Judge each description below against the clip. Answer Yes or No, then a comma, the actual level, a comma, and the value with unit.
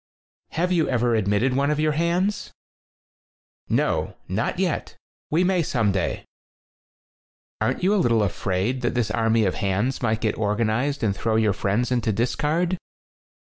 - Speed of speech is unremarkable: Yes, average, 160 wpm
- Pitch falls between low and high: No, low, 120 Hz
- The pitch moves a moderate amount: No, wide, 5.8 semitones